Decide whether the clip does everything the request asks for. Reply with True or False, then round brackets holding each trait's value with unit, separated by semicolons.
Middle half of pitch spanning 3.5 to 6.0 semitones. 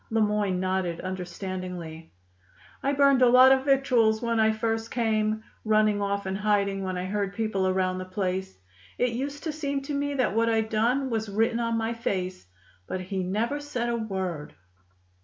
True (4.0 semitones)